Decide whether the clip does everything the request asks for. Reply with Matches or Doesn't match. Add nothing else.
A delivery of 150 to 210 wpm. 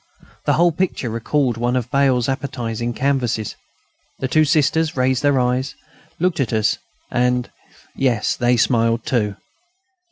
Doesn't match